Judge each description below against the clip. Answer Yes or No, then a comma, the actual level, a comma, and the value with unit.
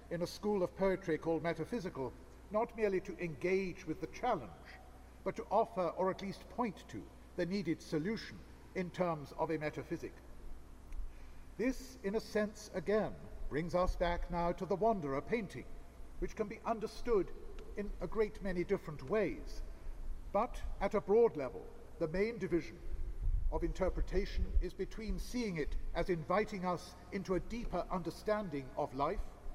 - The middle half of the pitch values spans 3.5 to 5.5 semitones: Yes, average, 4.6 semitones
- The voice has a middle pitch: Yes, medium, 180 Hz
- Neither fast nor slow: Yes, average, 155 wpm